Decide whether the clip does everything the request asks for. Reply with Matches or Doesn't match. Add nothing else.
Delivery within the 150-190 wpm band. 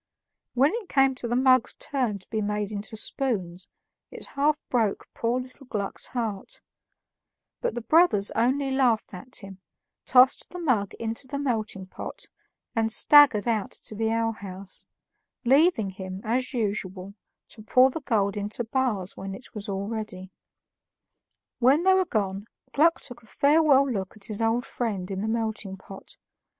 Matches